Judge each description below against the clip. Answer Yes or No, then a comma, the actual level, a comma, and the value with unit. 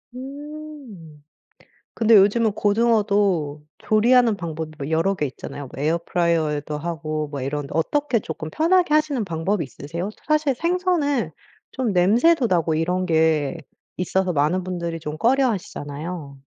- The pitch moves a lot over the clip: Yes, wide, 7.2 semitones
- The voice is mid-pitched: Yes, medium, 180 Hz